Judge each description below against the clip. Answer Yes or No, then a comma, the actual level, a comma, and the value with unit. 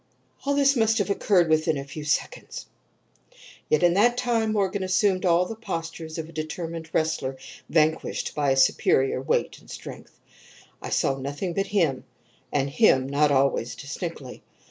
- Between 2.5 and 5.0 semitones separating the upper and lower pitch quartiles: No, wide, 5.6 semitones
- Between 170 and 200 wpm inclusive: No, average, 155 wpm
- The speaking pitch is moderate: Yes, medium, 165 Hz